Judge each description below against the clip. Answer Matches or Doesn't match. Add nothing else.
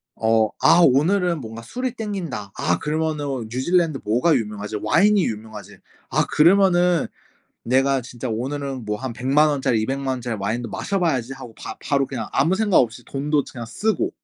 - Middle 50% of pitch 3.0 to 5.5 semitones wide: Doesn't match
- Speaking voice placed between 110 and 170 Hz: Matches